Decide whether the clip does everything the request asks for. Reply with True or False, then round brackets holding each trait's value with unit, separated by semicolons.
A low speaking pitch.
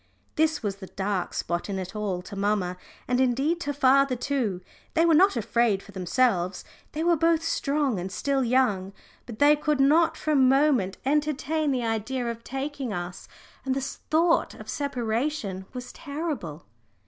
False (260 Hz)